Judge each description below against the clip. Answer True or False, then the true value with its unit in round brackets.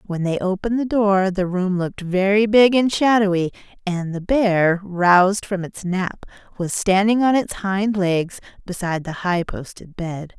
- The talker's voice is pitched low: False (190 Hz)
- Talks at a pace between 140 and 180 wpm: True (175 wpm)